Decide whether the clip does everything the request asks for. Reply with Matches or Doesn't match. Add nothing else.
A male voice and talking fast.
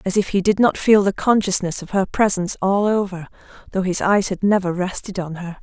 Doesn't match